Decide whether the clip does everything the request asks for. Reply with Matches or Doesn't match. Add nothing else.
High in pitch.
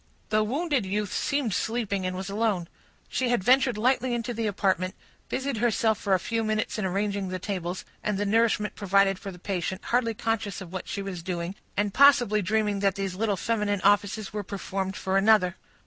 Matches